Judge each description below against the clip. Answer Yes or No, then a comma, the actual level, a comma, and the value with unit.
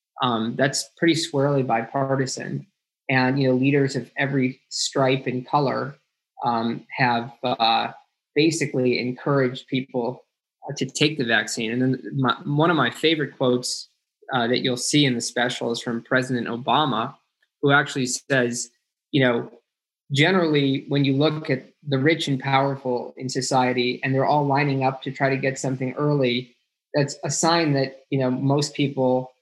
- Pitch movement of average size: No, narrow, 2.0 semitones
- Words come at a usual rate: Yes, average, 160 wpm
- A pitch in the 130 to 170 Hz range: Yes, low, 135 Hz